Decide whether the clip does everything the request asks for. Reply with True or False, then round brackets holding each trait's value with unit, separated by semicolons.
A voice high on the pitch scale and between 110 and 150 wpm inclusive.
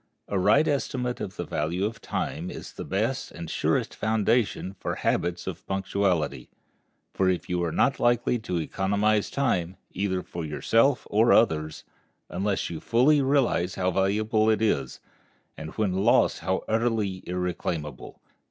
False (95 Hz; 145 wpm)